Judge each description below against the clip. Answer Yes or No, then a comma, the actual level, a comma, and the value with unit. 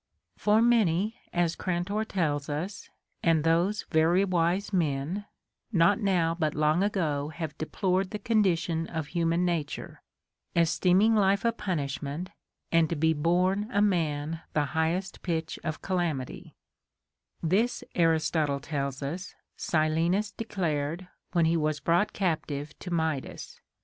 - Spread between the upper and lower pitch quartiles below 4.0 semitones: Yes, average, 3.4 semitones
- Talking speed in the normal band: No, slow, 130 wpm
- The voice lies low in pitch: No, medium, 170 Hz